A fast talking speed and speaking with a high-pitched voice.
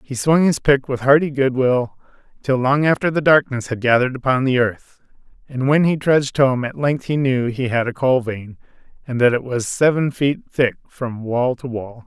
No: fast, 215 wpm; low, 130 Hz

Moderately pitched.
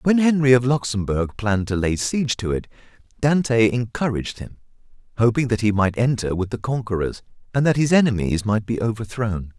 No: low, 115 Hz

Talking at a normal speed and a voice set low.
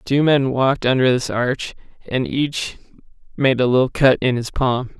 Yes: average, 190 wpm; low, 130 Hz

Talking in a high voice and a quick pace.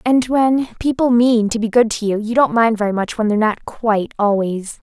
Yes: high, 225 Hz; fast, 220 wpm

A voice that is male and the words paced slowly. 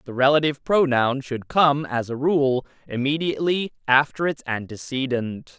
Yes: male; slow, 130 wpm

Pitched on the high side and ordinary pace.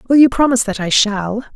No: high, 230 Hz; fast, 230 wpm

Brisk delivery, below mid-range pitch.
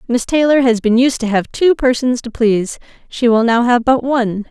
No: fast, 225 wpm; high, 240 Hz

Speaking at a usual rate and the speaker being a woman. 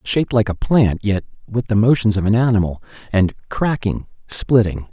No: average, 170 wpm; male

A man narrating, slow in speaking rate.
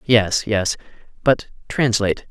Yes: male; slow, 80 wpm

